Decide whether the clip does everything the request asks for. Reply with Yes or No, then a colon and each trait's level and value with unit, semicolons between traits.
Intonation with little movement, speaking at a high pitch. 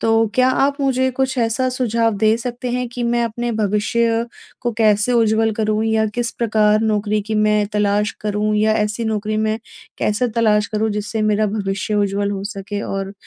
Yes: narrow, 1.9 semitones; high, 215 Hz